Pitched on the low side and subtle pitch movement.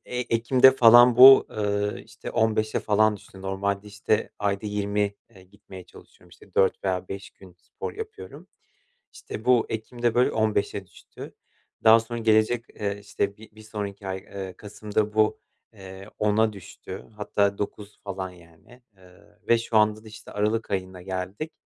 Yes: low, 105 Hz; narrow, 2.3 semitones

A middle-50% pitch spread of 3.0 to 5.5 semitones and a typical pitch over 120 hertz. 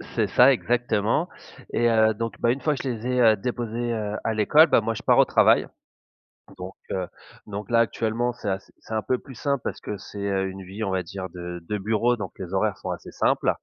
No: average, 3.4 semitones; low, 110 Hz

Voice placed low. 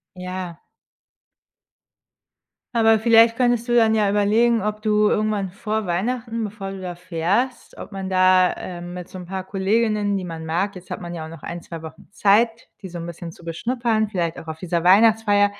No: high, 195 Hz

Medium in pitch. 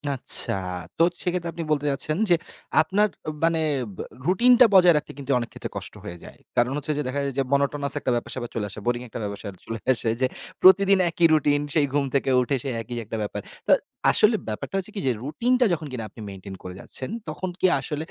Yes: medium, 145 Hz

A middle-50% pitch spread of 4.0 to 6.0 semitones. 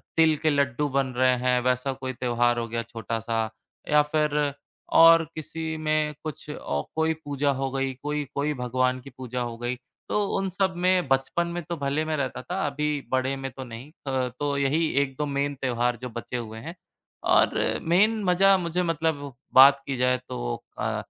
No: average, 3.5 semitones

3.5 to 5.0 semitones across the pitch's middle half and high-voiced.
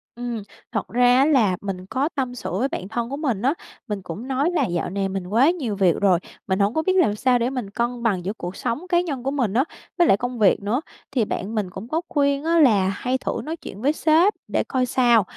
No: wide, 5.6 semitones; high, 240 Hz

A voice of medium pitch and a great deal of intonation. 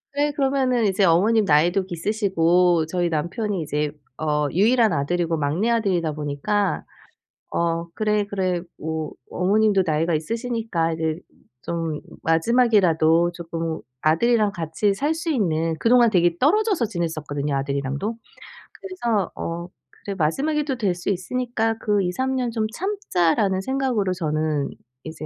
Yes: medium, 180 Hz; wide, 5.8 semitones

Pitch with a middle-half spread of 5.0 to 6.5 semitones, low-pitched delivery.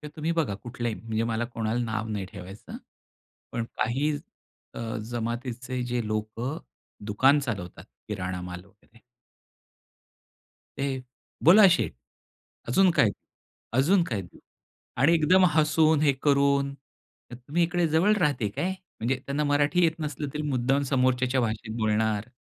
Yes: average, 5.3 semitones; low, 130 Hz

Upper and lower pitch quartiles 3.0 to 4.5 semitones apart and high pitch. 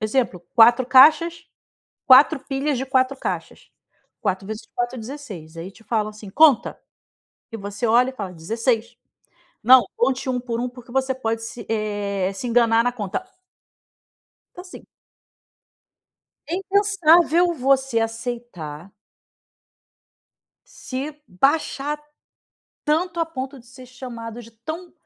Yes: average, 3.7 semitones; high, 245 Hz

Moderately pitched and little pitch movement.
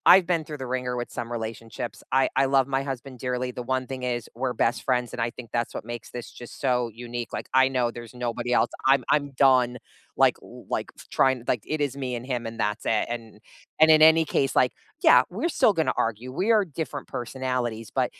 No: low, 125 Hz; narrow, 2.3 semitones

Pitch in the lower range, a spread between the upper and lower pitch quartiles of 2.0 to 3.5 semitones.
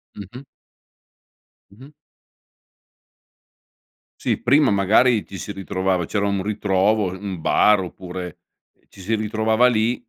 Yes: low, 105 Hz; average, 2.7 semitones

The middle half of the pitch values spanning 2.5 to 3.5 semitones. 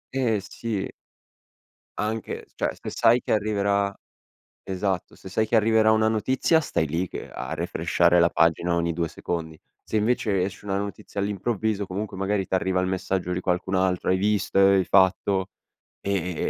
Yes: average, 2.8 semitones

